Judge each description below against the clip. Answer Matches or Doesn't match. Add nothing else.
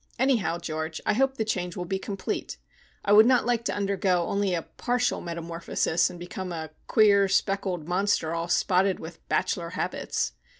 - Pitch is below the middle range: Doesn't match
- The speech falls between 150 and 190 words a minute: Matches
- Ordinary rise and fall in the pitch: Matches